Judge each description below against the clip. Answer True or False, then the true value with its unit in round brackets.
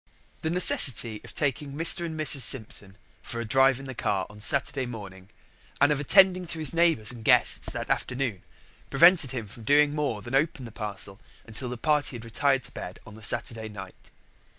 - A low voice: True (130 Hz)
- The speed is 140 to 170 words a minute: False (195 wpm)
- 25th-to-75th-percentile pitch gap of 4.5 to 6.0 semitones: True (5.1 semitones)